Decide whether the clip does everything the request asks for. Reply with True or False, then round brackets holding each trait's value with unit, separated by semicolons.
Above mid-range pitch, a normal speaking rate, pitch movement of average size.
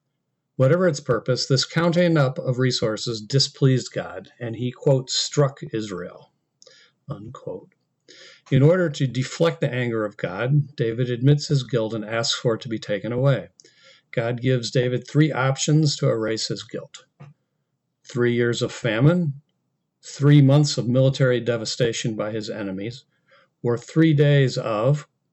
False (135 Hz; 145 wpm; 3.6 semitones)